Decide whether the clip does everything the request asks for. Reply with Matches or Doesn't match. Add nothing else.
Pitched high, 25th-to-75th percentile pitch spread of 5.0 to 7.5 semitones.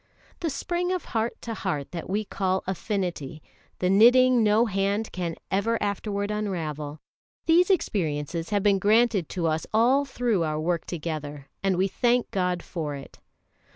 Matches